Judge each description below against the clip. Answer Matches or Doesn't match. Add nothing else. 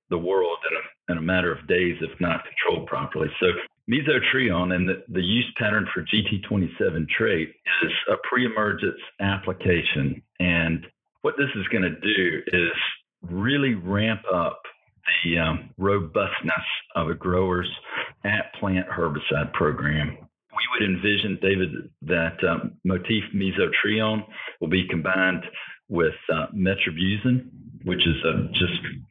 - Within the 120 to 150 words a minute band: Matches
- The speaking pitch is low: Matches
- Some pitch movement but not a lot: Matches